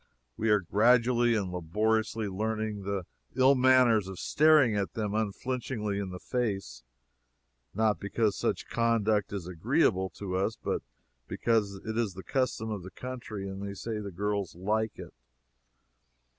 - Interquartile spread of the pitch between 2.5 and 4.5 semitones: Yes, average, 2.8 semitones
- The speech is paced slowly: No, average, 145 wpm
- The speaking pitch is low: Yes, low, 105 Hz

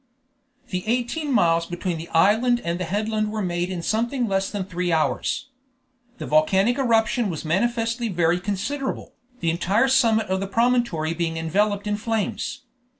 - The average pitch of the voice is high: Yes, high, 205 Hz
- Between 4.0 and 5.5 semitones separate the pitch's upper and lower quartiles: Yes, average, 5.1 semitones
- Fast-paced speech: No, average, 155 wpm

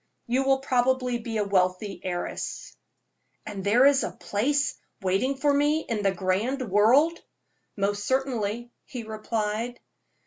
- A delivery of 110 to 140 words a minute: Yes, slow, 135 wpm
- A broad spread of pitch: No, average, 4.6 semitones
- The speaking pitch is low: No, high, 235 Hz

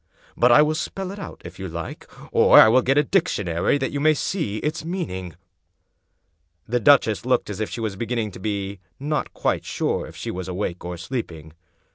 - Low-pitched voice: Yes, low, 115 Hz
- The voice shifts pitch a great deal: Yes, wide, 7.8 semitones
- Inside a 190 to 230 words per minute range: Yes, average, 195 wpm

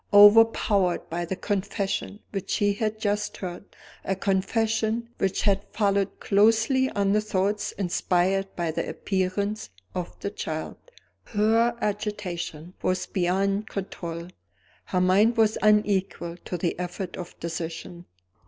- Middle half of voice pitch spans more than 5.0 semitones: No, average, 2.7 semitones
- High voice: Yes, high, 195 Hz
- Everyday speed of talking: No, slow, 125 wpm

